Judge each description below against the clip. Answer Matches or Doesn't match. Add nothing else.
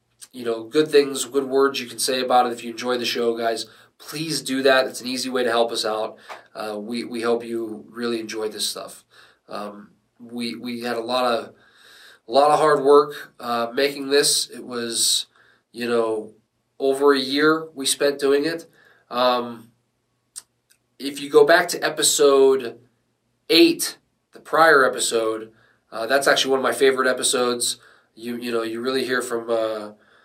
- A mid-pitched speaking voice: Doesn't match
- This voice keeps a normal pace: Matches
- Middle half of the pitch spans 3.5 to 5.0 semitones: Doesn't match